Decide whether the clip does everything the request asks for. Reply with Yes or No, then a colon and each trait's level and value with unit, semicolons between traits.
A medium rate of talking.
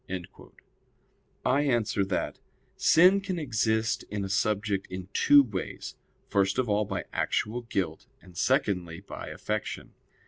No: slow, 130 wpm